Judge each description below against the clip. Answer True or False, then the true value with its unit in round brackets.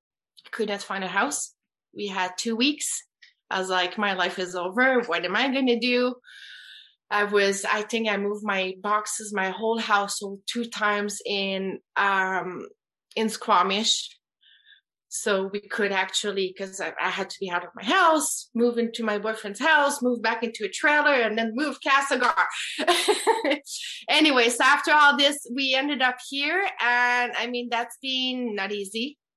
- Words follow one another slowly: False (170 wpm)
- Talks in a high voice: True (230 Hz)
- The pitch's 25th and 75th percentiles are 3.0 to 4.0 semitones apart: False (4.9 semitones)